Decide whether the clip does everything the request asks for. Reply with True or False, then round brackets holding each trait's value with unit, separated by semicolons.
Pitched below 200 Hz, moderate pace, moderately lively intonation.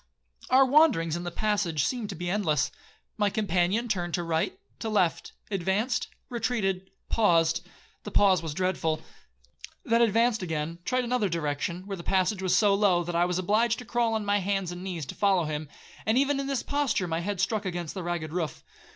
True (190 Hz; 185 wpm; 4.2 semitones)